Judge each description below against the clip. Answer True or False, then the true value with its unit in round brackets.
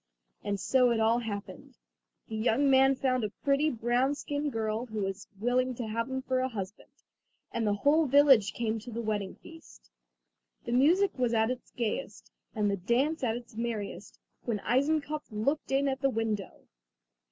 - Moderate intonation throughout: True (3.6 semitones)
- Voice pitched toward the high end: True (240 Hz)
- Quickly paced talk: False (175 wpm)